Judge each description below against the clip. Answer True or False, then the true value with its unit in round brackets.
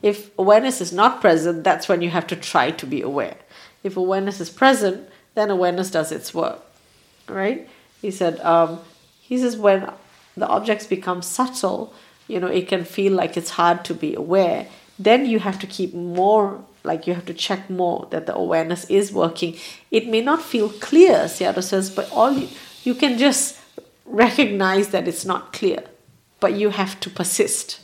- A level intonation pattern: False (3.5 semitones)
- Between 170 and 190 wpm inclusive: True (185 wpm)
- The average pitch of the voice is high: True (195 Hz)